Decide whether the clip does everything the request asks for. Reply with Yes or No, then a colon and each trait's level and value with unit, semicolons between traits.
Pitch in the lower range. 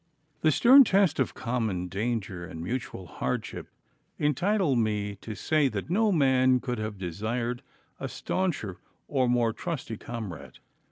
Yes: low, 120 Hz